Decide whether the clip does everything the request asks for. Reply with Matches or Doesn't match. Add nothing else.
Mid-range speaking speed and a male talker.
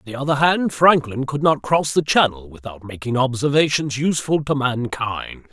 Matches